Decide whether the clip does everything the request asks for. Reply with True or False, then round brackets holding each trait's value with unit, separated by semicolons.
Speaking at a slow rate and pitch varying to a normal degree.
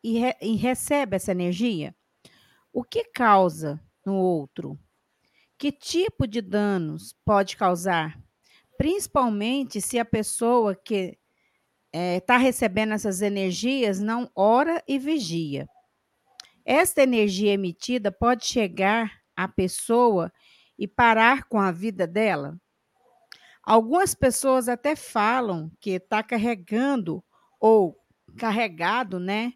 True (110 wpm; 4.7 semitones)